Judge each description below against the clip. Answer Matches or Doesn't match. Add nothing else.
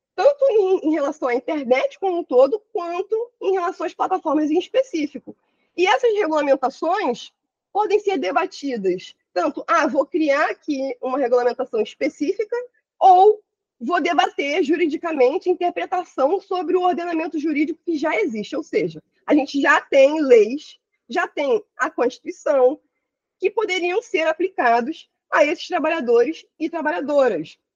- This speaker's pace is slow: Doesn't match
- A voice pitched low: Doesn't match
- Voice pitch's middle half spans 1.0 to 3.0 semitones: Doesn't match